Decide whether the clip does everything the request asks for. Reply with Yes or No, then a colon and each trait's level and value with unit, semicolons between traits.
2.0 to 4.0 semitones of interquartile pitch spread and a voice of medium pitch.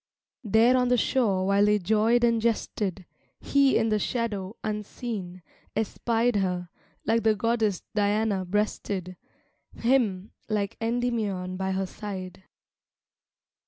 No: average, 3.3 semitones; high, 210 Hz